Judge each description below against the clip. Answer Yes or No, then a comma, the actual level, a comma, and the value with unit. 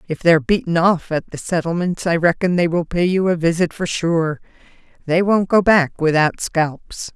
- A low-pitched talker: No, medium, 170 Hz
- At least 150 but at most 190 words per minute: No, average, 200 wpm